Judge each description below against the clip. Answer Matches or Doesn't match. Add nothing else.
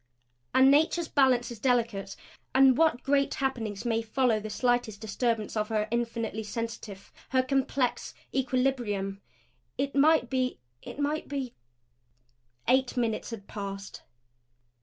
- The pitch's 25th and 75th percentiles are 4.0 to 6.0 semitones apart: Doesn't match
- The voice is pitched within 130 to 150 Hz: Doesn't match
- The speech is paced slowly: Matches